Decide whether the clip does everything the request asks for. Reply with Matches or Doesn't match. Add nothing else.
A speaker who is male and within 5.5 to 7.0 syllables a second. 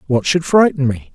Doesn't match